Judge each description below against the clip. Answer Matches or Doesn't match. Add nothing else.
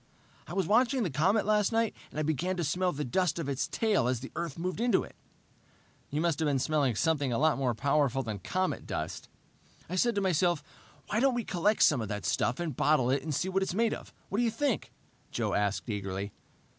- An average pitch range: Doesn't match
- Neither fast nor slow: Doesn't match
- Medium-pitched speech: Matches